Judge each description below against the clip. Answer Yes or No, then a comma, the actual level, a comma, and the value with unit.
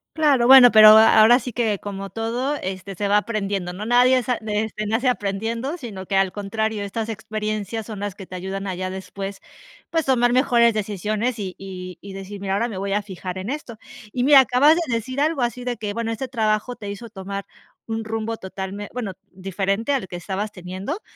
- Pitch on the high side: Yes, high, 215 Hz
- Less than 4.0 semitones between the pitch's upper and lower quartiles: Yes, average, 3.5 semitones